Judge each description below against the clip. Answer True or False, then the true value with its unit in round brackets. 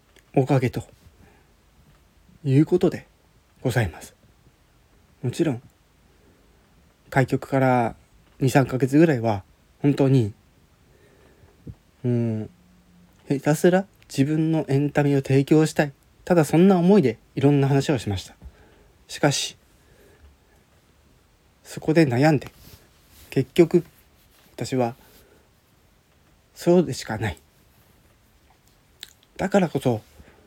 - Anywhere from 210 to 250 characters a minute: False (185 characters per minute)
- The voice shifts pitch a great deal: True (7.1 semitones)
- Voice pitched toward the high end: False (130 Hz)